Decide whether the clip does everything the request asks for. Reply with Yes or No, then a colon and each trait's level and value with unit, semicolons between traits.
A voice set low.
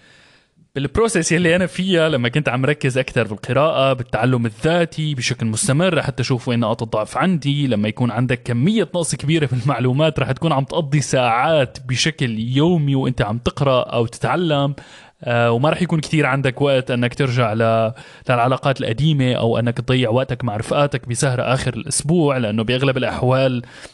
Yes: low, 130 Hz